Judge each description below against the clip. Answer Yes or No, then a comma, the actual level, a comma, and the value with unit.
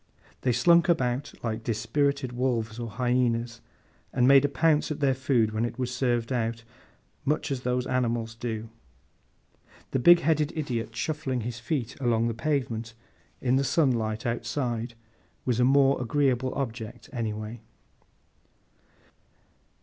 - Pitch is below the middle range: Yes, low, 125 Hz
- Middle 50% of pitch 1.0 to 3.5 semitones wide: Yes, average, 2.9 semitones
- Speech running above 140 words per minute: No, slow, 135 wpm